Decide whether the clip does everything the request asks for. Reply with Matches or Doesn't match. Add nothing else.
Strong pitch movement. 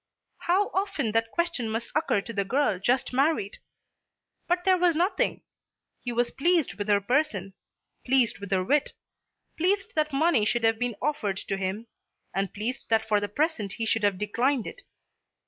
Matches